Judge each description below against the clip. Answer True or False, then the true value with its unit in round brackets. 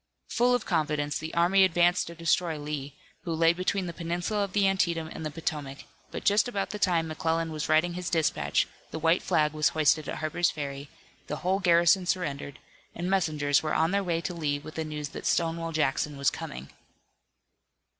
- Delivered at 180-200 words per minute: True (195 wpm)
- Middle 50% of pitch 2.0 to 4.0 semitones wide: True (2.7 semitones)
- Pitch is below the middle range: False (165 Hz)